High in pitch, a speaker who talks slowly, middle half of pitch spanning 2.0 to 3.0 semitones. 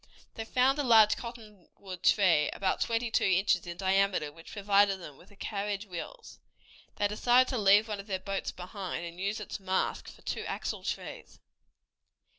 No: high, 200 Hz; average, 175 wpm; average, 2.7 semitones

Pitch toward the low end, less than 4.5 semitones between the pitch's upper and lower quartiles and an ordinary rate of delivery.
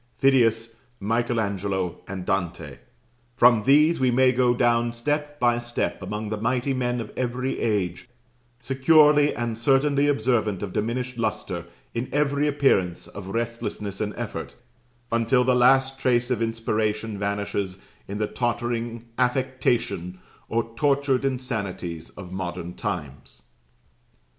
No: low, 120 Hz; average, 3.8 semitones; slow, 130 wpm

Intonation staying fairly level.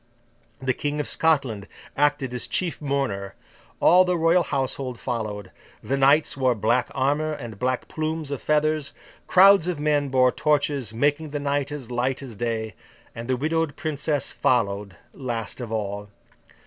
No: average, 4.0 semitones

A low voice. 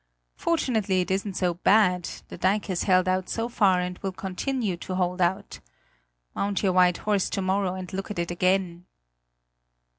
No: medium, 185 Hz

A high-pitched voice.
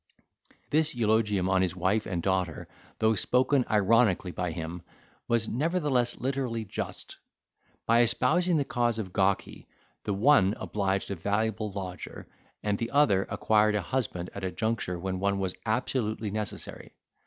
No: low, 105 Hz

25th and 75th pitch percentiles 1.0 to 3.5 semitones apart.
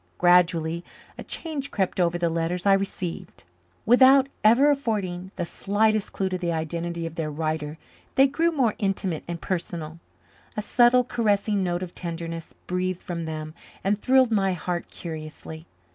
No: average, 4.4 semitones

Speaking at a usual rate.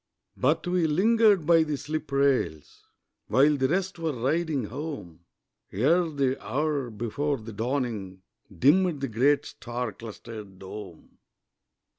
No: slow, 125 wpm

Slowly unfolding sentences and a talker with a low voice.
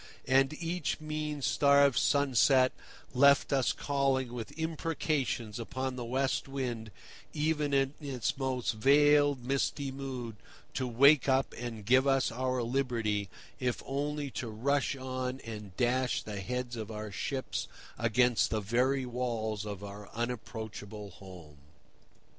Yes: slow, 130 wpm; low, 130 Hz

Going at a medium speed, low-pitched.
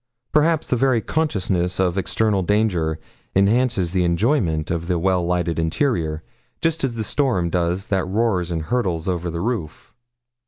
Yes: average, 155 wpm; very low, 95 Hz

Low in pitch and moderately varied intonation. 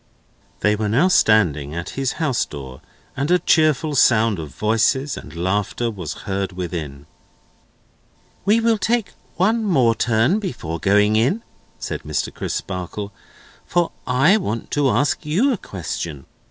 No: low, 115 Hz; wide, 8.9 semitones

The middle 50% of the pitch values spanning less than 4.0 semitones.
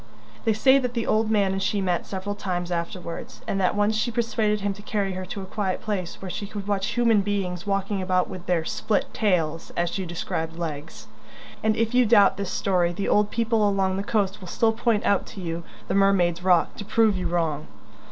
Yes: average, 2.8 semitones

